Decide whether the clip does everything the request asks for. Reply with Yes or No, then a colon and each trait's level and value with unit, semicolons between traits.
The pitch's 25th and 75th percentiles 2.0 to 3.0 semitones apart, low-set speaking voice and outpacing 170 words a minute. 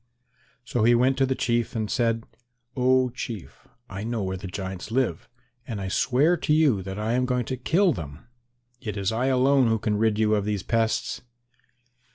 No: average, 3.7 semitones; low, 115 Hz; average, 195 wpm